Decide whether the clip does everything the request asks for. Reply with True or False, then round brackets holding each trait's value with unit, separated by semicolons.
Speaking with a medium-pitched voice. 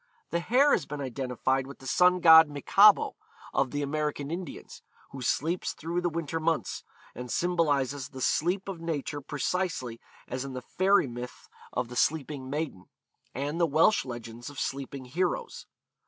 True (145 Hz)